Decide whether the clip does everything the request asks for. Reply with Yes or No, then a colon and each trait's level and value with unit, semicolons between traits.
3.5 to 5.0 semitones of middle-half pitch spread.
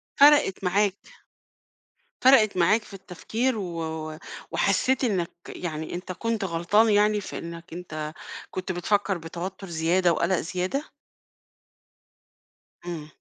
Yes: average, 3.8 semitones